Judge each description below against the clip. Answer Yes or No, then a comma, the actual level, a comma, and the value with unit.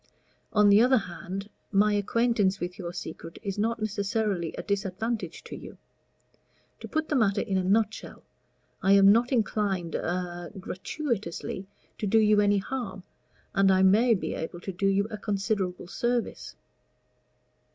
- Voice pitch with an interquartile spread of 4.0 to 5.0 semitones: No, average, 2.7 semitones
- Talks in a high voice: Yes, high, 200 Hz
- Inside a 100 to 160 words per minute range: Yes, average, 150 wpm